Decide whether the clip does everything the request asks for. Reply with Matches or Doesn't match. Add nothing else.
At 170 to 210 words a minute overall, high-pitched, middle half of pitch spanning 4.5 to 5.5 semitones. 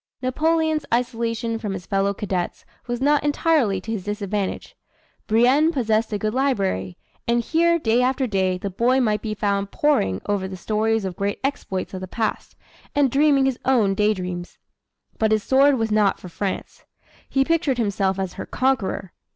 Matches